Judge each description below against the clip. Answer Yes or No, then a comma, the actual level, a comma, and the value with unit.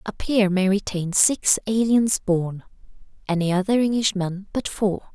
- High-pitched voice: Yes, high, 200 Hz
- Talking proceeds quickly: No, average, 140 wpm